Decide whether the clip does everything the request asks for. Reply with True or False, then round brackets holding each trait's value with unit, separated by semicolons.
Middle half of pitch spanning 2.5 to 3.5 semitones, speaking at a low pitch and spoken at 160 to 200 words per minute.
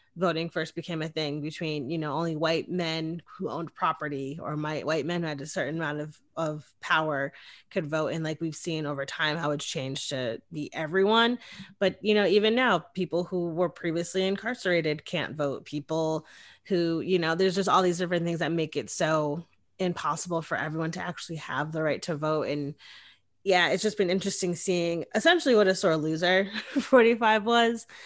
False (3.2 semitones; 165 Hz; 190 wpm)